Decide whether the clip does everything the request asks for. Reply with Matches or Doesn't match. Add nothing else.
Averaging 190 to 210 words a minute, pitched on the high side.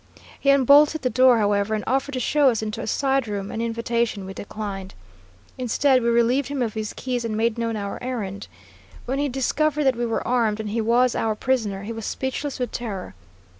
Matches